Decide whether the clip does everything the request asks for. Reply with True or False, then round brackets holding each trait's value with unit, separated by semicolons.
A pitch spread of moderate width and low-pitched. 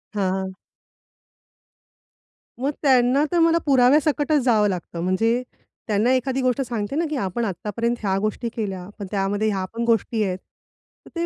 False (4.9 semitones; 230 Hz)